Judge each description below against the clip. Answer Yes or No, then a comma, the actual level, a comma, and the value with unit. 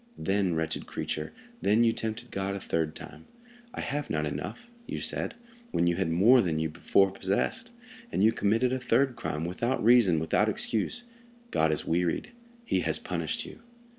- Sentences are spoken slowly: No, average, 175 wpm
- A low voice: Yes, low, 100 Hz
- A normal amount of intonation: No, wide, 6.4 semitones